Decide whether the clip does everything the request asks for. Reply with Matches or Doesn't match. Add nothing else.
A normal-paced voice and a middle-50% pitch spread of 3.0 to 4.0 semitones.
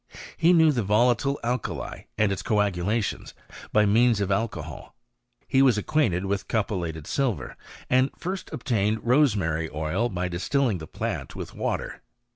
Doesn't match